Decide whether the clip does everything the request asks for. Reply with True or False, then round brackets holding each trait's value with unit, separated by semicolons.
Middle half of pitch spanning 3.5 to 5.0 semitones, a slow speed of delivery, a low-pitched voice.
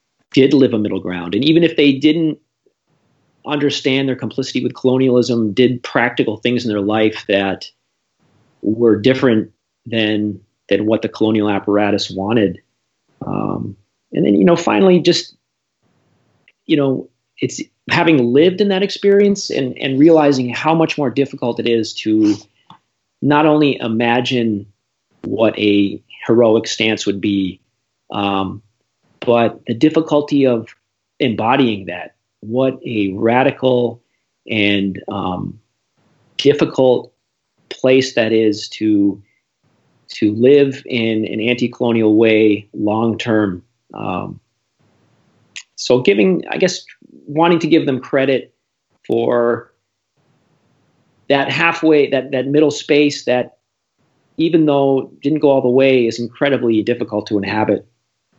True (4.6 semitones; 125 wpm; 120 Hz)